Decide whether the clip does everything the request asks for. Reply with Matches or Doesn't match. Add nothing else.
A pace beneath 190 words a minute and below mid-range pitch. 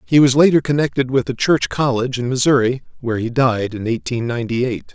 Doesn't match